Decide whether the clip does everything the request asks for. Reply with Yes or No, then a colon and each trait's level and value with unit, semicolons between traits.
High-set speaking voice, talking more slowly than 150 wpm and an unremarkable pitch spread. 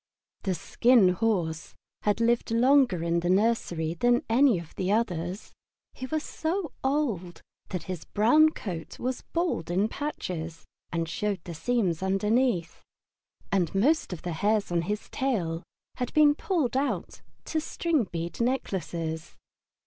No: high, 205 Hz; average, 140 wpm; wide, 6.9 semitones